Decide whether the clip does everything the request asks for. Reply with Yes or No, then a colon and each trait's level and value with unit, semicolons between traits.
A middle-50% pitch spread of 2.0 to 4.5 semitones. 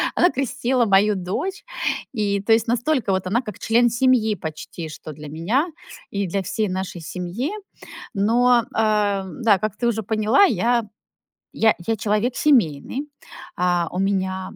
Yes: average, 4.1 semitones